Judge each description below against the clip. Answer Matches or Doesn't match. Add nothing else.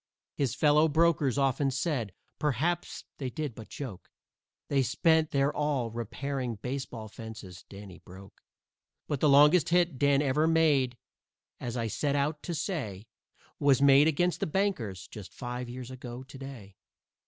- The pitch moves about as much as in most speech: Matches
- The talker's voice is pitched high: Doesn't match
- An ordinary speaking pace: Matches